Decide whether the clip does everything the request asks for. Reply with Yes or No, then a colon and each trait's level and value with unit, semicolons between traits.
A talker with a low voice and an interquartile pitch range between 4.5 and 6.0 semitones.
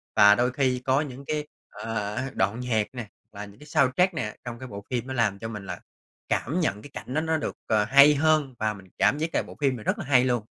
Yes: low, 125 Hz; average, 5.0 semitones